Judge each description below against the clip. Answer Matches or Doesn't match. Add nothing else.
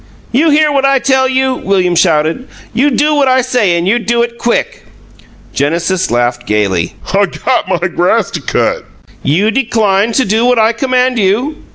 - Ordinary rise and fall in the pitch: Doesn't match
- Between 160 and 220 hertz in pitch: Doesn't match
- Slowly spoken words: Doesn't match